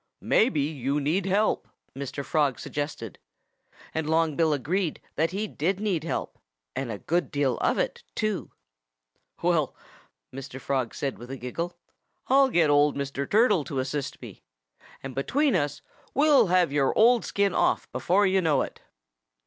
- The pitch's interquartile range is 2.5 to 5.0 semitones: No, wide, 5.6 semitones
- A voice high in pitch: No, medium, 155 Hz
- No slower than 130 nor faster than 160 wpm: Yes, average, 155 wpm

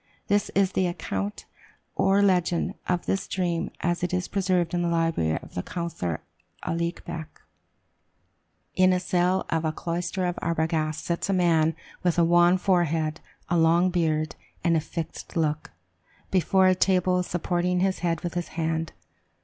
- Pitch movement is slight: Yes, narrow, 1.9 semitones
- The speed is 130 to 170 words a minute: Yes, average, 155 wpm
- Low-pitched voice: No, medium, 175 Hz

